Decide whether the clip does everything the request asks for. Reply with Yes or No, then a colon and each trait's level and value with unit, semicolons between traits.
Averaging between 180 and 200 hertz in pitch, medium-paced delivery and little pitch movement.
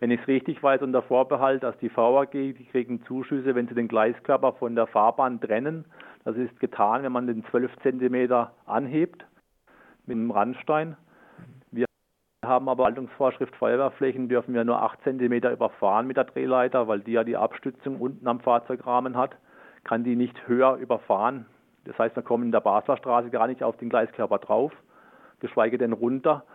No: low, 125 Hz; average, 175 wpm; narrow, 1.8 semitones